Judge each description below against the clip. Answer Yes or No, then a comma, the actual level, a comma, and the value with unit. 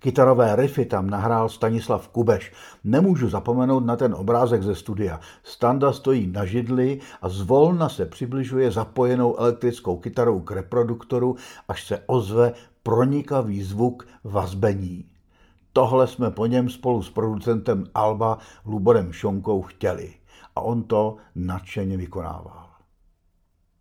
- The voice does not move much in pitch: No, average, 4.4 semitones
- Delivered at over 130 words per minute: No, average, 120 wpm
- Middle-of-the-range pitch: No, low, 115 Hz